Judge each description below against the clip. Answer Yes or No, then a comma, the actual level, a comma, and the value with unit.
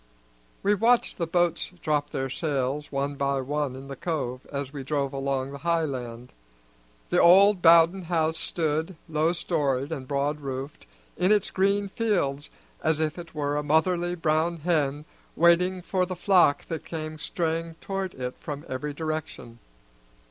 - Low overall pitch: No, medium, 155 Hz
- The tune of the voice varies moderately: Yes, average, 3.7 semitones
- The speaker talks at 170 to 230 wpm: No, average, 160 wpm